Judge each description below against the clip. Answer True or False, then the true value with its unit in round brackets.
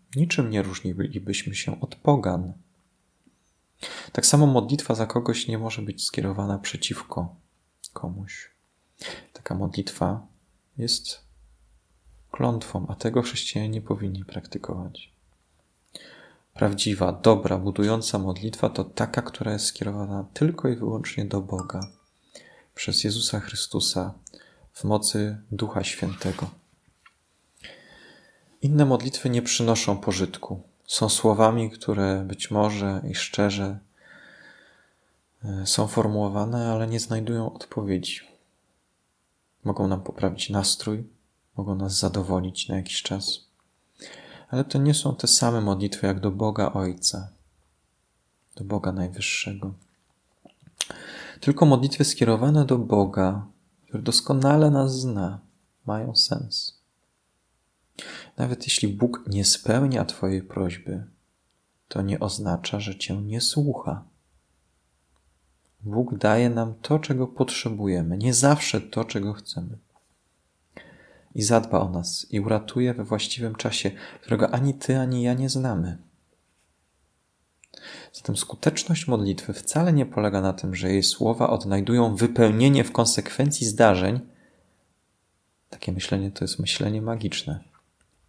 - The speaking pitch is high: False (105 Hz)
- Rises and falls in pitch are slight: False (3.7 semitones)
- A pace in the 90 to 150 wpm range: True (110 wpm)